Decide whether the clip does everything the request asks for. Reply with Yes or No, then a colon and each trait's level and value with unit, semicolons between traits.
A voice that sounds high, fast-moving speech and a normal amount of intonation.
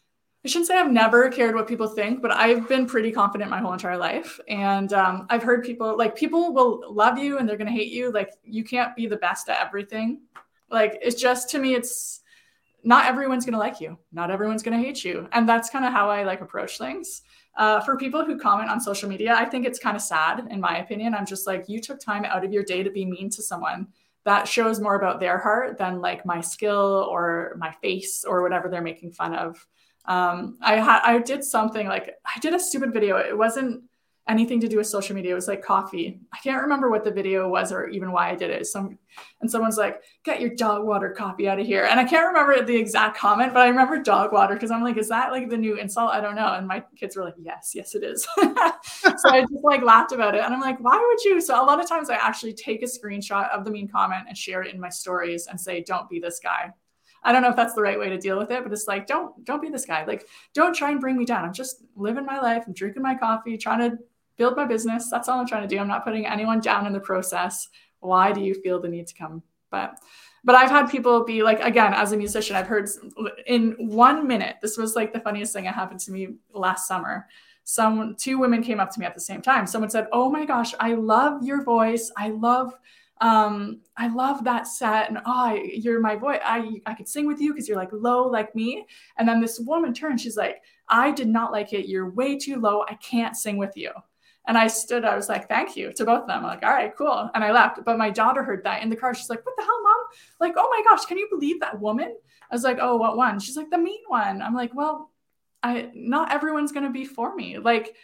Yes: high, 225 Hz; fast, 255 wpm; average, 4.0 semitones